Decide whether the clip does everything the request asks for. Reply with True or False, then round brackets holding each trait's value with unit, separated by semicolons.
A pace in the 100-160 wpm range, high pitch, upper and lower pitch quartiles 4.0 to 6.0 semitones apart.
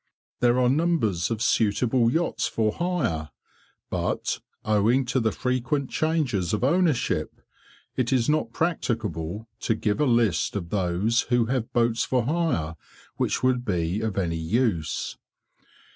False (140 wpm; 115 Hz; 4.3 semitones)